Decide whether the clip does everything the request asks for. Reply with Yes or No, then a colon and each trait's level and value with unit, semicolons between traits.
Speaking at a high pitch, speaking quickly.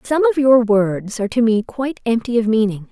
Yes: high, 230 Hz; fast, 225 wpm